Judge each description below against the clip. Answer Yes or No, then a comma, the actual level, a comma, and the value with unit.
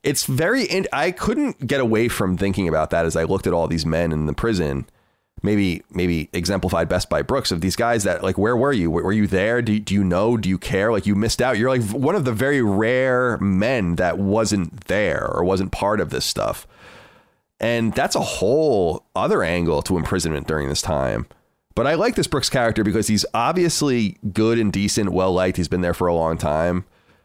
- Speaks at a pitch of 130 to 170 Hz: No, low, 100 Hz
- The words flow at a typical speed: No, fast, 215 wpm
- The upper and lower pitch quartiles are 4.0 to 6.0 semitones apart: Yes, average, 4.6 semitones